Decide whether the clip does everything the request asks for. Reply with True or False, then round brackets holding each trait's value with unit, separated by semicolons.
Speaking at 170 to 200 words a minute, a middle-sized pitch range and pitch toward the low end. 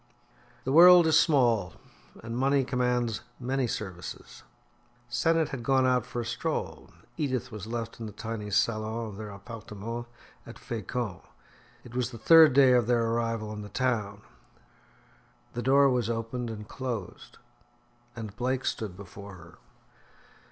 False (145 wpm; 3.0 semitones; 115 Hz)